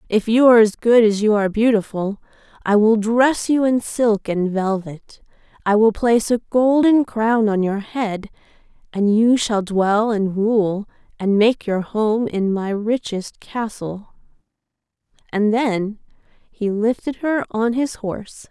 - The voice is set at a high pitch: Yes, high, 220 Hz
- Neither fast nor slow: Yes, average, 155 wpm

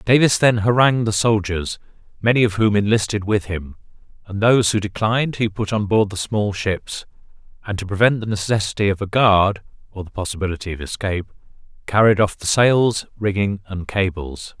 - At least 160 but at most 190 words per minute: Yes, average, 175 wpm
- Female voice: No, male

